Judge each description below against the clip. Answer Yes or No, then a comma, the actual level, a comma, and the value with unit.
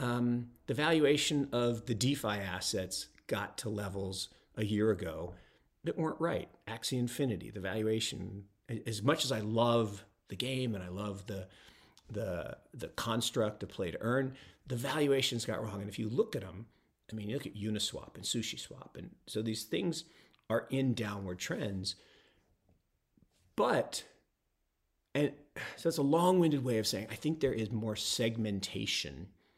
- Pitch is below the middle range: Yes, low, 110 Hz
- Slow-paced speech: No, average, 160 wpm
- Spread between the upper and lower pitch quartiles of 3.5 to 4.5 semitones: Yes, average, 4.2 semitones